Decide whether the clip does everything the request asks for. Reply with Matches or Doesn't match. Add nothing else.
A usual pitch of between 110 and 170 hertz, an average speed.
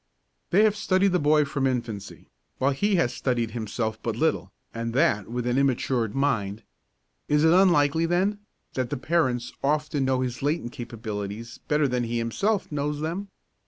Matches